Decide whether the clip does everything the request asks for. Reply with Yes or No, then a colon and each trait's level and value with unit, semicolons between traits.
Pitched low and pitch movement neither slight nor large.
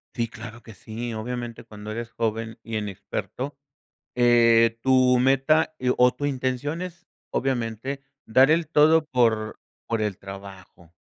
Yes: low, 120 Hz; average, 3.2 semitones